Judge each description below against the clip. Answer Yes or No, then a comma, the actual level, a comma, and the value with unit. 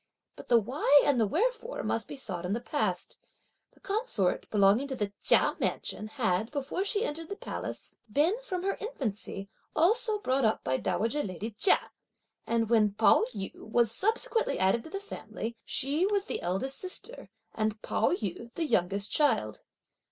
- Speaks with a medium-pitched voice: No, high, 245 Hz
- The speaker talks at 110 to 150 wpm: No, average, 170 wpm